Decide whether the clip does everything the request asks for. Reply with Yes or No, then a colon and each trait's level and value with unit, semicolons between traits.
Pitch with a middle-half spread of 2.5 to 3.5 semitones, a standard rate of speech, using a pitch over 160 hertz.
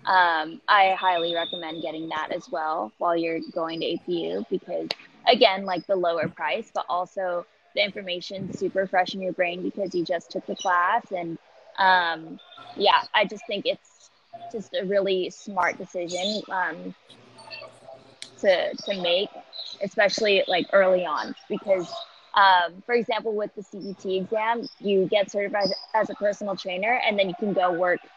Yes: average, 2.9 semitones; average, 160 wpm; high, 190 Hz